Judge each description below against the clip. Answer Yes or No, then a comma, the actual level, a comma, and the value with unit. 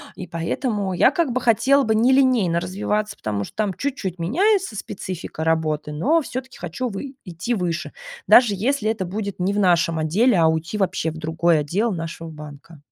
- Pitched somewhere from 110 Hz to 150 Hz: No, high, 190 Hz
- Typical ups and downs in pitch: No, wide, 6.3 semitones